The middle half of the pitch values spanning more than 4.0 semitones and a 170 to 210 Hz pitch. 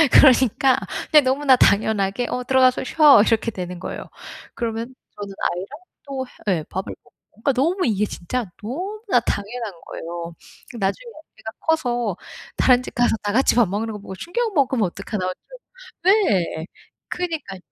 No: wide, 5.5 semitones; high, 240 Hz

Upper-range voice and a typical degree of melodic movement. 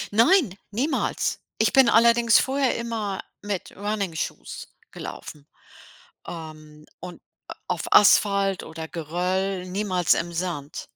Yes: high, 195 Hz; average, 4.9 semitones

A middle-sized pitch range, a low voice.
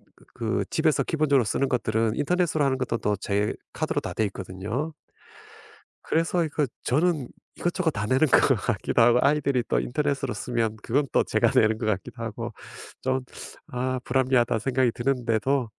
Yes: average, 4.1 semitones; low, 125 Hz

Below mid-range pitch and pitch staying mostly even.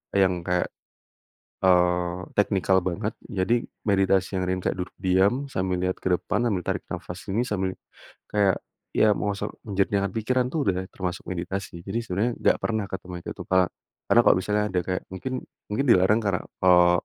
Yes: very low, 95 Hz; narrow, 2.1 semitones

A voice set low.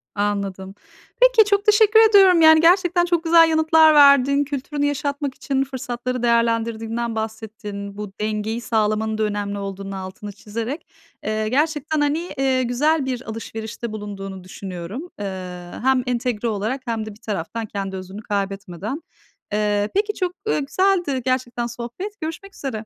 No: high, 235 Hz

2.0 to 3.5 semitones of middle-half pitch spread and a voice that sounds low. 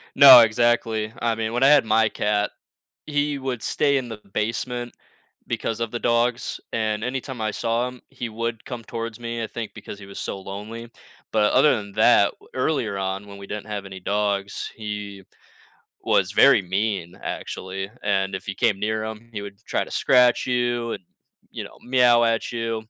Yes: average, 2.7 semitones; low, 110 Hz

